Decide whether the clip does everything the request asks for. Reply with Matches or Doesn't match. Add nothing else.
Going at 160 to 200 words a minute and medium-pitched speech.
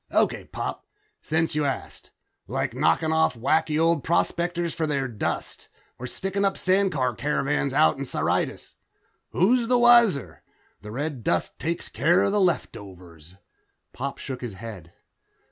Doesn't match